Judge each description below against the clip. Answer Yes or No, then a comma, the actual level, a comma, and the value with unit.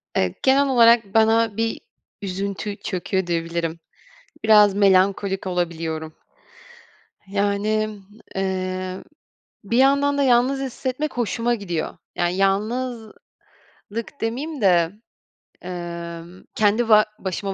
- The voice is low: No, high, 200 Hz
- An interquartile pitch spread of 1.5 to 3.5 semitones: No, average, 4.0 semitones